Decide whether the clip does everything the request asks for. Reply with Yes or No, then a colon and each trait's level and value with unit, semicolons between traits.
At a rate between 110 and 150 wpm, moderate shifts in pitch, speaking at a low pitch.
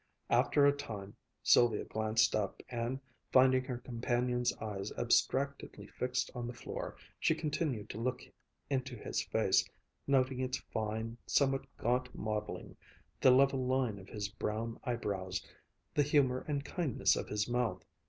Yes: average, 145 wpm; average, 3.2 semitones; low, 125 Hz